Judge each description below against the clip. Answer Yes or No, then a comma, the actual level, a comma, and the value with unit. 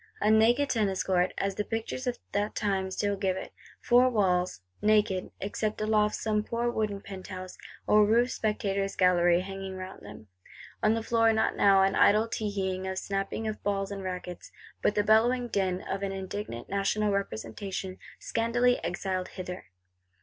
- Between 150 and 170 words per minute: Yes, average, 160 wpm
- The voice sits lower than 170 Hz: No, high, 200 Hz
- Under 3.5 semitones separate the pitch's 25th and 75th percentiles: Yes, narrow, 2.4 semitones